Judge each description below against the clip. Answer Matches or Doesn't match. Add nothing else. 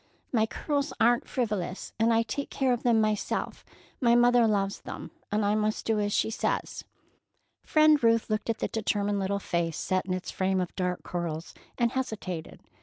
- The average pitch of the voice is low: Doesn't match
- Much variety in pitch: Doesn't match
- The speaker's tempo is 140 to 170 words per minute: Doesn't match